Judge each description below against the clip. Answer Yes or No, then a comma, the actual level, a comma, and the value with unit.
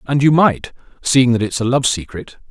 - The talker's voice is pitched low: Yes, low, 125 Hz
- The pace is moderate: Yes, average, 190 wpm